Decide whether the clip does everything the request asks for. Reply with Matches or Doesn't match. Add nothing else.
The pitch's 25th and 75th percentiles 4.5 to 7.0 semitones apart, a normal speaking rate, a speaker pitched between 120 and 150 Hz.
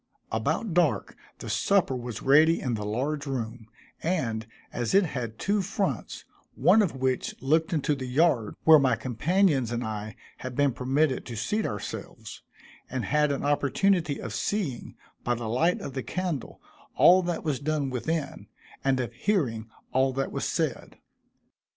Matches